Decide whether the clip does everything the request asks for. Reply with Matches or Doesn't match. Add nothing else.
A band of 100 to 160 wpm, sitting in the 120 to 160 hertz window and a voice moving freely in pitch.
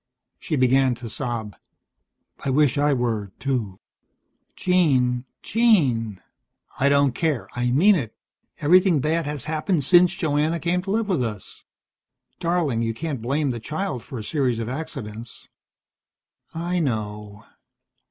Matches